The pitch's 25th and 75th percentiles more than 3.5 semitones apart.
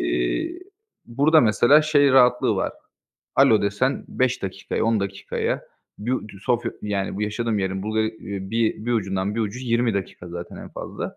Yes: average, 3.9 semitones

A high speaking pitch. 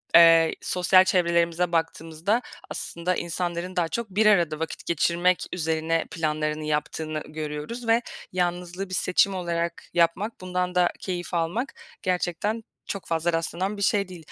No: medium, 175 Hz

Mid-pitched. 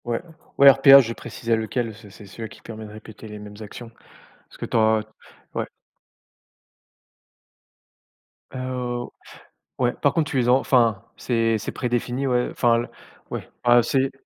No: low, 115 Hz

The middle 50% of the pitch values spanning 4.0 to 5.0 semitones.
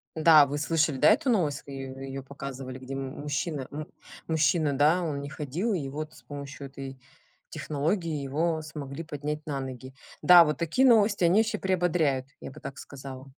No: average, 3.3 semitones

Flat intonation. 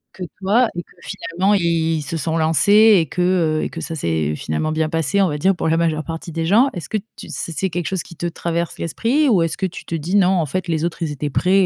No: average, 3.1 semitones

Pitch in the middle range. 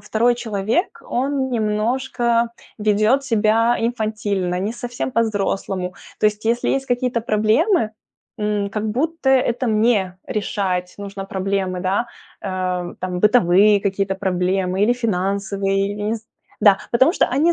No: high, 215 Hz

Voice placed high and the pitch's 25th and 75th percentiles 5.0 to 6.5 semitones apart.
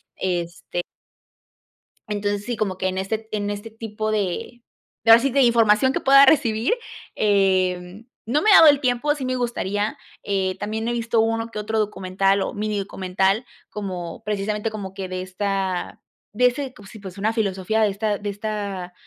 No: high, 210 Hz; average, 2.8 semitones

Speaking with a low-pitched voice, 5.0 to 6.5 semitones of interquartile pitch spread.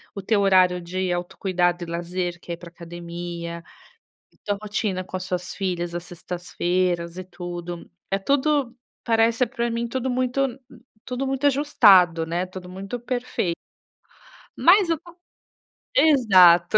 No: medium, 185 Hz; wide, 5.4 semitones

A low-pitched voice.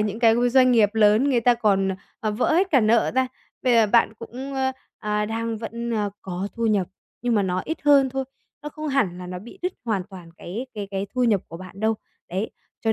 No: high, 225 Hz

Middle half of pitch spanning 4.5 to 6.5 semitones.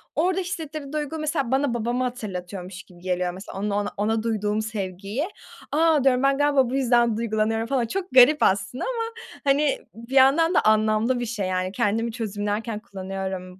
Yes: average, 5.2 semitones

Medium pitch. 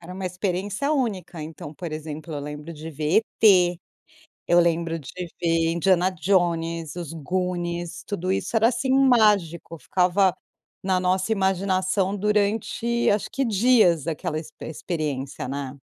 Yes: medium, 180 Hz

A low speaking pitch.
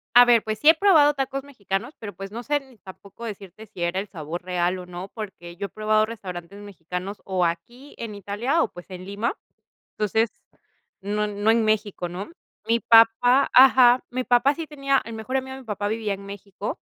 No: high, 215 Hz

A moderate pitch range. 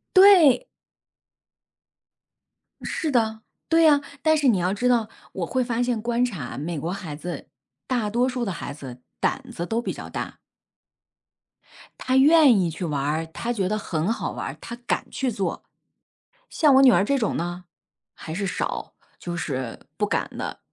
No: wide, 6.8 semitones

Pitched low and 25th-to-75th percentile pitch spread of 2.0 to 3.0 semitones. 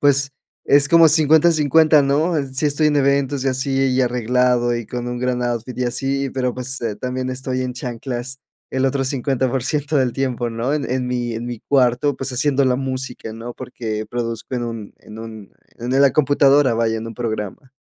Yes: low, 130 Hz; narrow, 2.4 semitones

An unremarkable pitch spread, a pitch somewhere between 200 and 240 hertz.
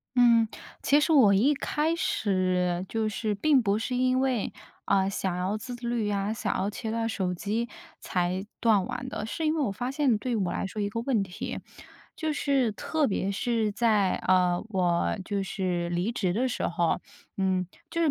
Yes: average, 4.6 semitones; high, 215 Hz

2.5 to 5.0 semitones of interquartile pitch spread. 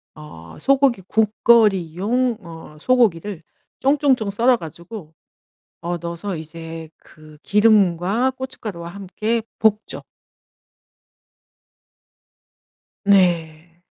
No: wide, 5.4 semitones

